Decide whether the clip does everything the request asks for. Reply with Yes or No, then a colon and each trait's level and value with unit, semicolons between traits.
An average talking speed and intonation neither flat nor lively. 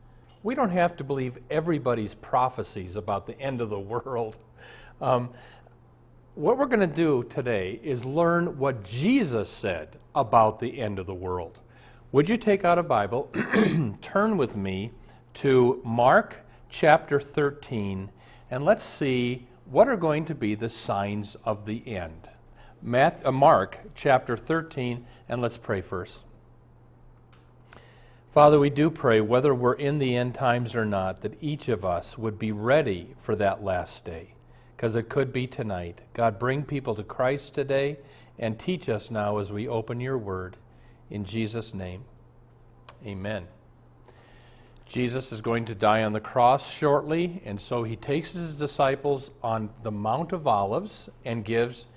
Yes: average, 155 wpm; average, 4.1 semitones